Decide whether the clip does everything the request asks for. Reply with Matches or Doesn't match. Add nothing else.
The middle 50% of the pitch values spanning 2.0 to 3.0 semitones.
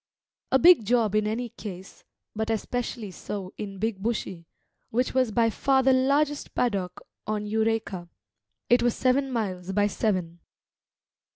Doesn't match